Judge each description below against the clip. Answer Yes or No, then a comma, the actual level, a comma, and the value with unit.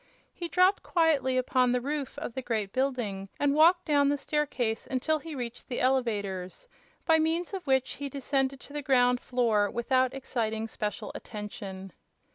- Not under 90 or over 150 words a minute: No, average, 165 wpm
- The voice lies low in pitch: No, very high, 260 Hz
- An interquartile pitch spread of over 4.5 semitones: No, average, 4.0 semitones